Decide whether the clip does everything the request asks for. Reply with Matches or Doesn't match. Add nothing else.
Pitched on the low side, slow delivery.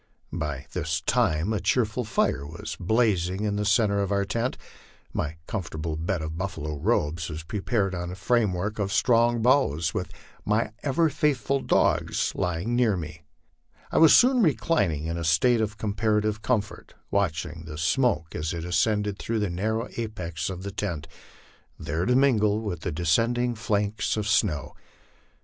Doesn't match